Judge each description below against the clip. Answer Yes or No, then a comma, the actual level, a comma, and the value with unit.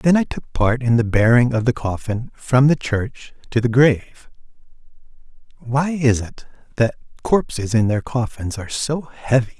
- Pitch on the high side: No, low, 120 Hz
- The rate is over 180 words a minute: No, average, 170 wpm